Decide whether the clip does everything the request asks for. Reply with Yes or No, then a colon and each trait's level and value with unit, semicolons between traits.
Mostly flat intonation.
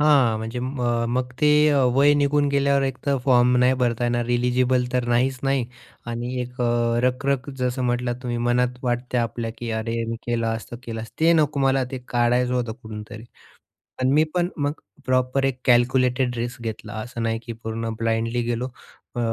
Yes: narrow, 1.9 semitones